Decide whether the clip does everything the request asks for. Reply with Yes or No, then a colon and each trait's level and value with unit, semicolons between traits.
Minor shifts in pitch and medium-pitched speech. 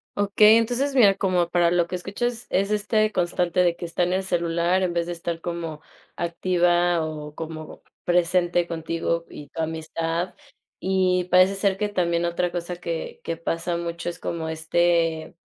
Yes: narrow, 1.7 semitones; medium, 175 Hz